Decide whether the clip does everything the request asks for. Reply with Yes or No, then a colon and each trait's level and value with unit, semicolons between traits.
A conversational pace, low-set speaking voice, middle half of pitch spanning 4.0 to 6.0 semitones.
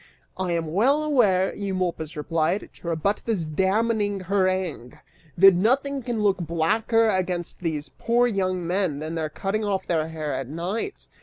No: average, 155 wpm; medium, 185 Hz; average, 4.4 semitones